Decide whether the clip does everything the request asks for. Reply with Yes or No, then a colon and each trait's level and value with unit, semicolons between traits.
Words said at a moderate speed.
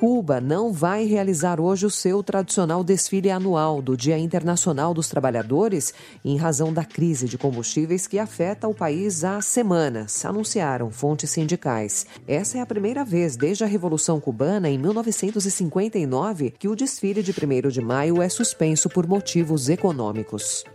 Yes: average, 155 wpm